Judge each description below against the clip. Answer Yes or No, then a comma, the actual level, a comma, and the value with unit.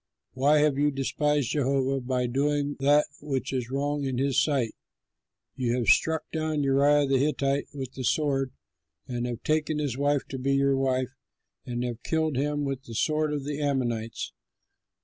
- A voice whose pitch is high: No, medium, 140 Hz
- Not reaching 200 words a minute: Yes, average, 170 wpm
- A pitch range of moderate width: No, narrow, 2.2 semitones